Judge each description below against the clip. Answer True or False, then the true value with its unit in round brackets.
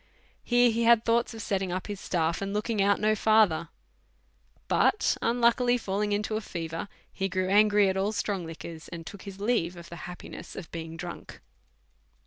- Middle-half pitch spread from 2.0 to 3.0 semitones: False (3.8 semitones)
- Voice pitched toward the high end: True (200 Hz)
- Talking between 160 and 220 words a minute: True (185 wpm)